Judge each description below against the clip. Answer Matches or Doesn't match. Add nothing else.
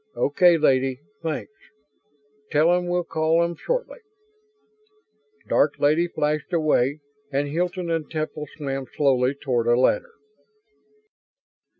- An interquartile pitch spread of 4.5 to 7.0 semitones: Doesn't match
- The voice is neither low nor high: Matches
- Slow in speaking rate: Matches